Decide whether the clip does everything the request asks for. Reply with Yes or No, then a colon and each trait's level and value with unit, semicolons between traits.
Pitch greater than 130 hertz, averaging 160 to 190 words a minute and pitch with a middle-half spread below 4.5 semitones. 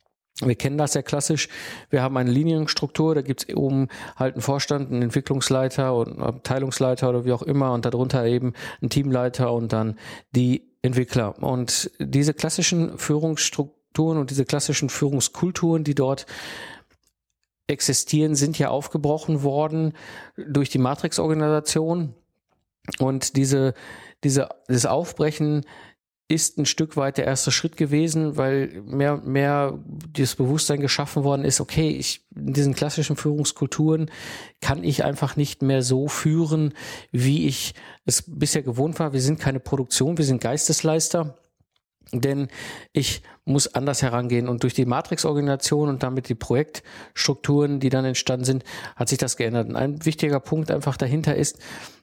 No: medium, 140 Hz; average, 150 wpm; narrow, 2.6 semitones